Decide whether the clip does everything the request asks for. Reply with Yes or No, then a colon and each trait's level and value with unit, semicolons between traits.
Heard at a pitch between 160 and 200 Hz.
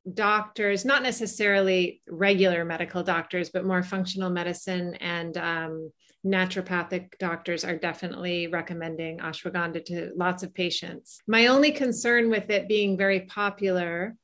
Yes: medium, 185 Hz